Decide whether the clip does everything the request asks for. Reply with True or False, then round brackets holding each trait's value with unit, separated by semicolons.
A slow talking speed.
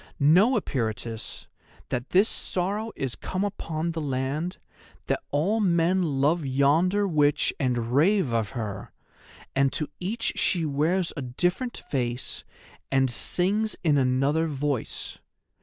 True (125 wpm)